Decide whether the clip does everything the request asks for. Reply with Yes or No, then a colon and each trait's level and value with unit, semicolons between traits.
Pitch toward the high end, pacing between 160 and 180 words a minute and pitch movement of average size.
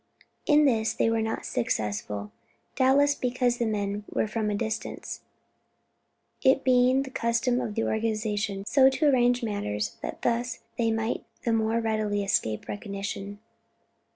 No: high, 225 Hz; average, 145 wpm; average, 3.2 semitones